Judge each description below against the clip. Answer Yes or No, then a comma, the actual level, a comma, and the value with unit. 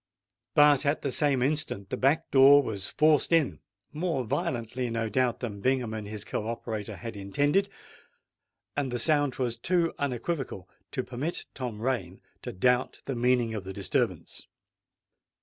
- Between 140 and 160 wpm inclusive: Yes, average, 150 wpm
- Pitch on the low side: Yes, low, 125 Hz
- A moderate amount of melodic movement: Yes, average, 4.5 semitones